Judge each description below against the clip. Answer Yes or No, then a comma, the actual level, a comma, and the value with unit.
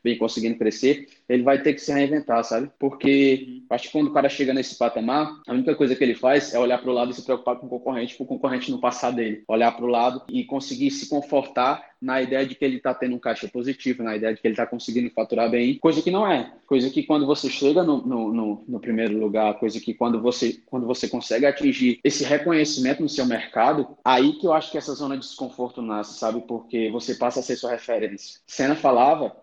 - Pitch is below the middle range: Yes, low, 125 Hz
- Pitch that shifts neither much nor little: Yes, average, 3.2 semitones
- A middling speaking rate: No, fast, 240 wpm